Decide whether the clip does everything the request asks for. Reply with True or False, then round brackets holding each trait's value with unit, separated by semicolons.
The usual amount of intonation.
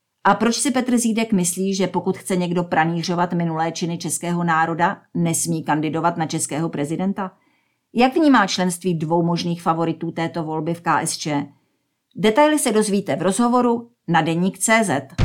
True (3.5 semitones)